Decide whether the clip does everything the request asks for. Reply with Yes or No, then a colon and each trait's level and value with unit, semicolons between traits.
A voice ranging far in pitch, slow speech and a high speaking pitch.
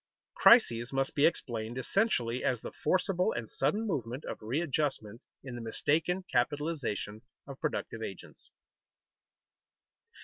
No: wide, 6.0 semitones; slow, 115 wpm; low, 135 Hz